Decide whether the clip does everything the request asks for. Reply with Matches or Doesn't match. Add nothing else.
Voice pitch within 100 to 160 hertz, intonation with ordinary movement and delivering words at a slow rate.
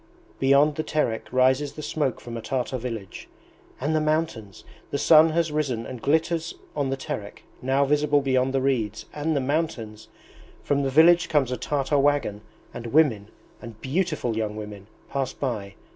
Doesn't match